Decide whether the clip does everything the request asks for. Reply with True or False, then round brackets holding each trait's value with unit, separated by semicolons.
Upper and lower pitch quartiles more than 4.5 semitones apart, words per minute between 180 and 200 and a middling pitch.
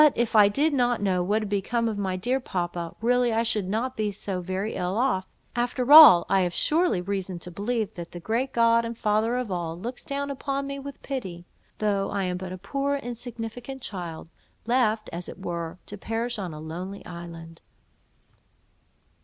False (5.1 semitones; 190 wpm; 210 Hz)